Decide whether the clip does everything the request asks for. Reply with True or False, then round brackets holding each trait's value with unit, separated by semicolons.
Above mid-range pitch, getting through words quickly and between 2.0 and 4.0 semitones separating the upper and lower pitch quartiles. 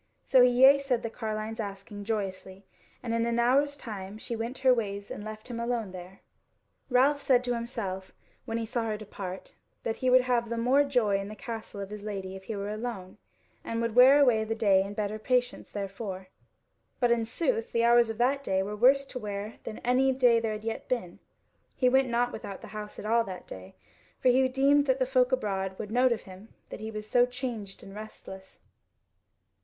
True (225 Hz; 215 wpm; 3.6 semitones)